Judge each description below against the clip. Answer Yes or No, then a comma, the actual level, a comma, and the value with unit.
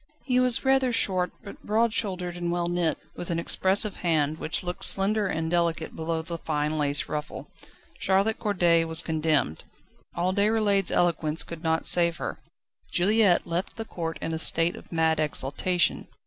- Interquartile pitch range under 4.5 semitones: Yes, average, 3.3 semitones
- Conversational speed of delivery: Yes, average, 165 wpm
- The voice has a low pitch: No, medium, 175 Hz